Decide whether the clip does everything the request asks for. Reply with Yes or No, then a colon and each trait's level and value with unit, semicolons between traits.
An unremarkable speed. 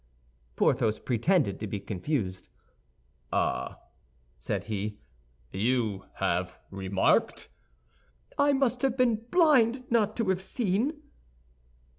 No: slow, 100 wpm